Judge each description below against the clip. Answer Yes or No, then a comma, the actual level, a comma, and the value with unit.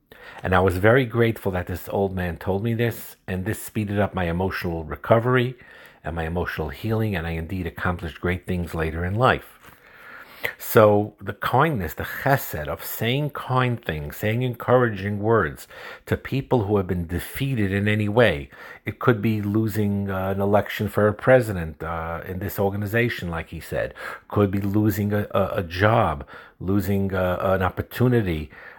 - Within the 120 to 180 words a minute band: Yes, average, 165 wpm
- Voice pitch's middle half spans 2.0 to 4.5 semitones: Yes, average, 3.8 semitones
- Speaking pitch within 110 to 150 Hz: No, low, 100 Hz